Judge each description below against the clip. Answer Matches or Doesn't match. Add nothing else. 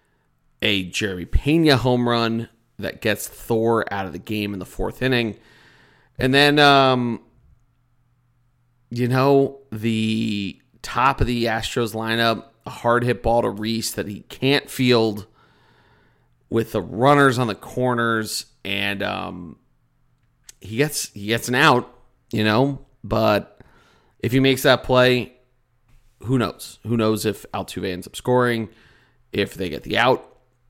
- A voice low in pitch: Matches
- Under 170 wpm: Matches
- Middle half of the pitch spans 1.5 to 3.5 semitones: Matches